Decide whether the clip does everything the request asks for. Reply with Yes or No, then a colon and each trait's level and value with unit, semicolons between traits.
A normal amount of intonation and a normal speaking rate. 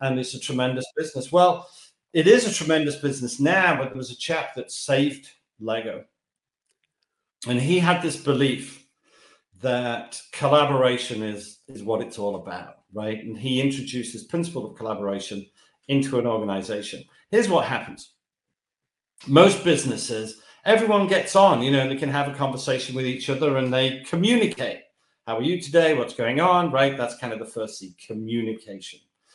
Yes: average, 4.8 semitones; average, 165 wpm